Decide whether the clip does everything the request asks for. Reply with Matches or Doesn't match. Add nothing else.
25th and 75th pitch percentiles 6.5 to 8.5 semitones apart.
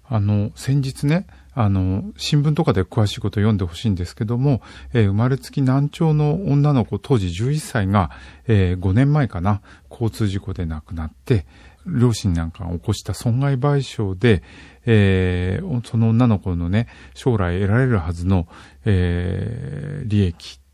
Doesn't match